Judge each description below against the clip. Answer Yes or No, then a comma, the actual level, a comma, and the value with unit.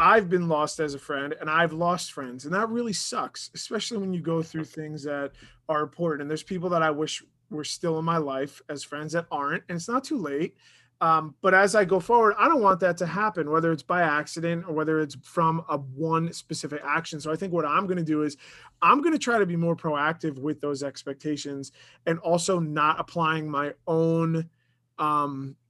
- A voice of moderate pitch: Yes, medium, 160 Hz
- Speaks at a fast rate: Yes, fast, 220 wpm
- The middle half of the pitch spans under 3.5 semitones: Yes, average, 2.9 semitones